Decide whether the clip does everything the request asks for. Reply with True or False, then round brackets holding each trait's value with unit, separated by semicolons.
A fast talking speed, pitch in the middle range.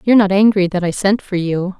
False (265 wpm; 195 Hz)